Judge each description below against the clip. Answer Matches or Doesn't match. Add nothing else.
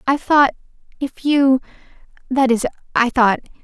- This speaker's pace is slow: Matches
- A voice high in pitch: Matches